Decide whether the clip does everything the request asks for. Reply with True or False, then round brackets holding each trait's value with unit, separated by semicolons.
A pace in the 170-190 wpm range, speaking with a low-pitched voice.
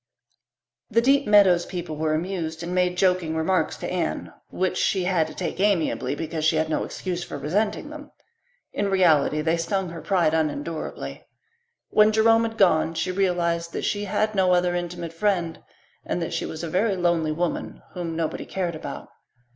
False (180 wpm; 175 Hz)